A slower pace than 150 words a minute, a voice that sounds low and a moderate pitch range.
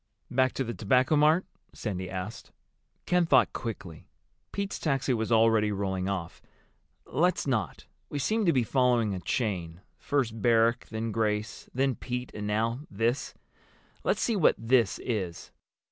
Yes: average, 140 wpm; low, 115 Hz; average, 4.0 semitones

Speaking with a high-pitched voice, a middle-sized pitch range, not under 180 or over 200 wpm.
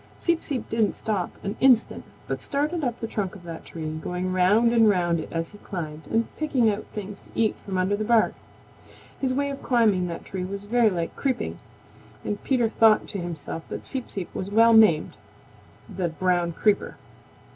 Yes: high, 205 Hz; average, 4.4 semitones; average, 190 wpm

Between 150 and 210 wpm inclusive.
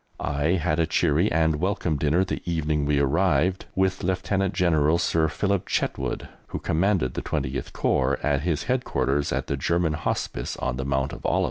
Yes: average, 175 wpm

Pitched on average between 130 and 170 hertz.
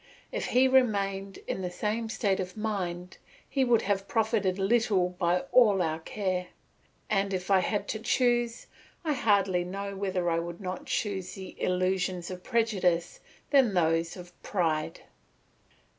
No: high, 195 Hz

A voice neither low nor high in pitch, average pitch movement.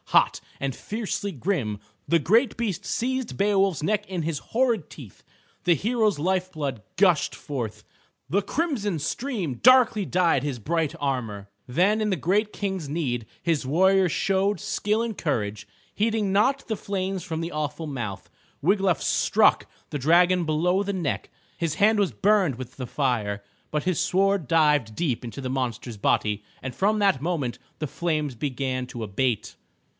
No: medium, 170 Hz; wide, 7.0 semitones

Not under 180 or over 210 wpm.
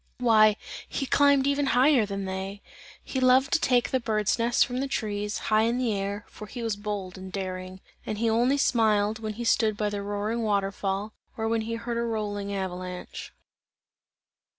Yes: average, 190 wpm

